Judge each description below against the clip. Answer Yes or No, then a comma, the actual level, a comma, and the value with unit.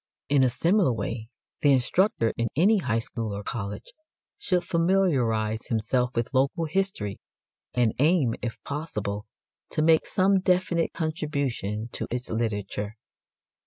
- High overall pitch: No, low, 125 Hz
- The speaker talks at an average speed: No, slow, 130 wpm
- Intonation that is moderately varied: No, wide, 6.9 semitones